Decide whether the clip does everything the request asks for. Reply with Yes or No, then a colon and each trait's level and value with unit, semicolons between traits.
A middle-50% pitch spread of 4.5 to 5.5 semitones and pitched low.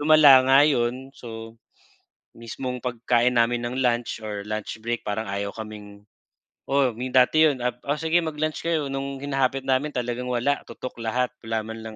No: average, 3.3 semitones; low, 125 Hz